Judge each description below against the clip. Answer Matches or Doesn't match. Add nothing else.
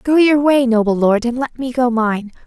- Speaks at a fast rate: Matches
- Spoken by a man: Doesn't match